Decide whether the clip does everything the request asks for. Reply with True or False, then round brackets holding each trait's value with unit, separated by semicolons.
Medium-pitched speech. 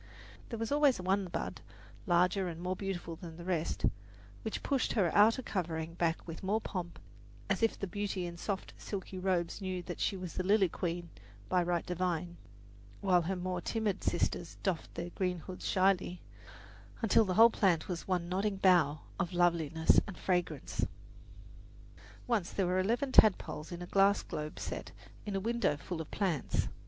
True (180 Hz)